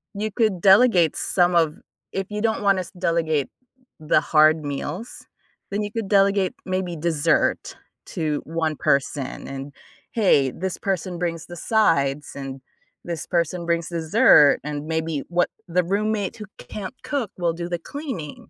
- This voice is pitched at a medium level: Yes, medium, 170 Hz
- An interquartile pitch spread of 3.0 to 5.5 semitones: Yes, average, 4.2 semitones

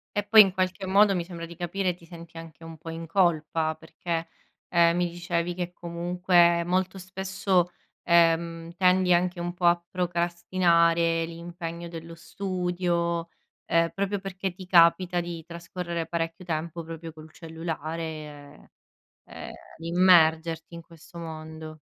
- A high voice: No, medium, 170 Hz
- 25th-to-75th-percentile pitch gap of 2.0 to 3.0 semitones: No, narrow, 1.5 semitones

